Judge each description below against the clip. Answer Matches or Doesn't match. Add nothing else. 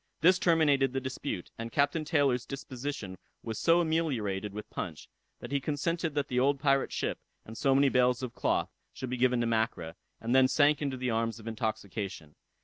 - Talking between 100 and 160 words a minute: Doesn't match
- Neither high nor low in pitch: Doesn't match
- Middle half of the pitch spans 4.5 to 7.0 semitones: Doesn't match